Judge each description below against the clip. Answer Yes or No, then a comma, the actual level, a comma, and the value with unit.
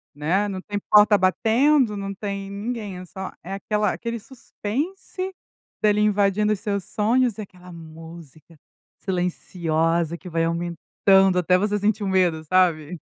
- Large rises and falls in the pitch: No, average, 3.3 semitones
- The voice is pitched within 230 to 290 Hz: No, high, 195 Hz